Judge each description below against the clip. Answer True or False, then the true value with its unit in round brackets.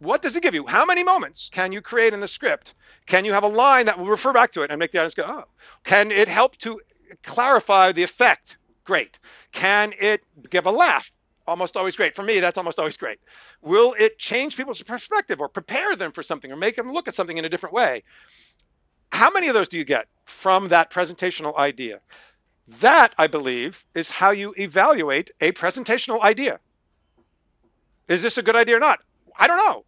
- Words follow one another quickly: True (210 wpm)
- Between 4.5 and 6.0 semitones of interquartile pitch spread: True (5.3 semitones)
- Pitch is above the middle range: True (205 Hz)